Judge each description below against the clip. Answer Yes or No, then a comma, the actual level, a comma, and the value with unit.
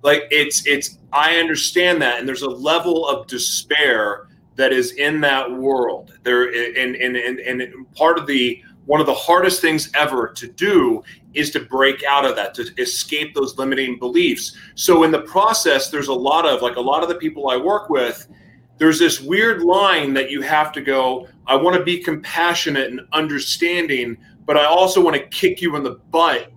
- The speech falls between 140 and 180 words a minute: No, average, 190 wpm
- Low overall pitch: No, medium, 150 Hz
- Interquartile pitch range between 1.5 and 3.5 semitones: No, average, 4.7 semitones